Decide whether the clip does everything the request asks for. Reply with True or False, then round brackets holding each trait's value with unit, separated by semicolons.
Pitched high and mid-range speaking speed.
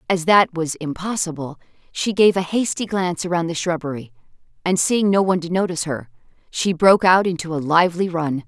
False (170 Hz; 185 wpm)